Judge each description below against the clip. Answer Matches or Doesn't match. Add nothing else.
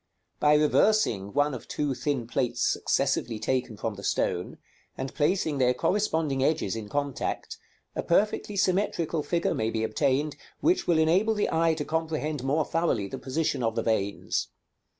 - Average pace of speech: Matches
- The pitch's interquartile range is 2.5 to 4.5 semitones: Doesn't match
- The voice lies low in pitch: Doesn't match